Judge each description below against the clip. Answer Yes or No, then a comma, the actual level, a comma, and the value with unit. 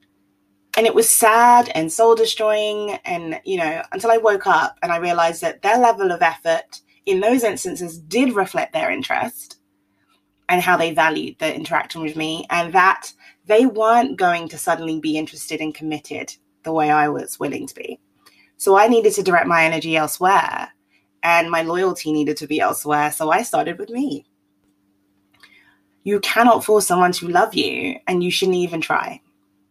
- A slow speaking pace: No, average, 175 wpm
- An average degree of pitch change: No, wide, 6.6 semitones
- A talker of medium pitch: Yes, medium, 170 Hz